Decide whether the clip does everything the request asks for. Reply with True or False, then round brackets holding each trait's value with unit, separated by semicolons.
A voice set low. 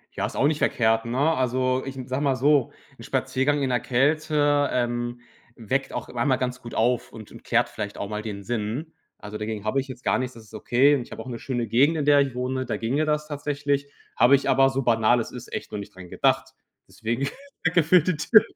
True (130 Hz)